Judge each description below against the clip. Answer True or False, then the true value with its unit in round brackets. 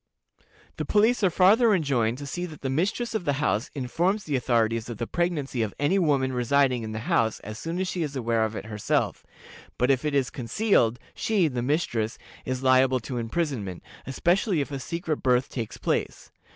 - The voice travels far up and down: True (6.4 semitones)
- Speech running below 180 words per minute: False (195 wpm)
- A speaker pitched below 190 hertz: True (135 Hz)